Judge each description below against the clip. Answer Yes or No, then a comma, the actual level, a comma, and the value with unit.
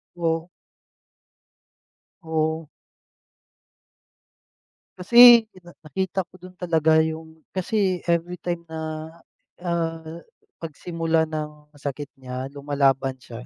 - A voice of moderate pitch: Yes, medium, 160 Hz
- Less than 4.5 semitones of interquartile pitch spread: Yes, narrow, 2.4 semitones